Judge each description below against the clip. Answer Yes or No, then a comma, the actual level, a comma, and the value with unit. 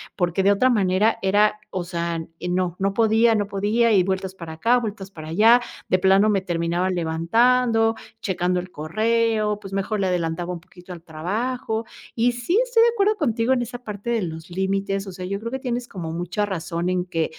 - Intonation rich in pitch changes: No, average, 4.3 semitones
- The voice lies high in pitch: Yes, high, 195 Hz